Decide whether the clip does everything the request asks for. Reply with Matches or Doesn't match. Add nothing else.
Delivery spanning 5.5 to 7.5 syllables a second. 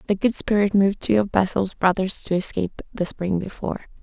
Matches